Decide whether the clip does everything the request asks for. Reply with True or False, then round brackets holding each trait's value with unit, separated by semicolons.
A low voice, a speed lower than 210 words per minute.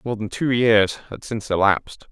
True (110 Hz; 200 wpm)